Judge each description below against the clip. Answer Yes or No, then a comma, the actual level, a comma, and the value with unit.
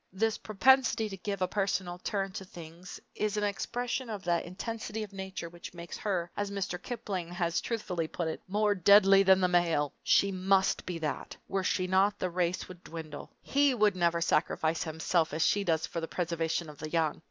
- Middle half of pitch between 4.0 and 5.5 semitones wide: No, average, 3.1 semitones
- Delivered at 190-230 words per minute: Yes, average, 200 wpm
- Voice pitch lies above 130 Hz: Yes, medium, 185 Hz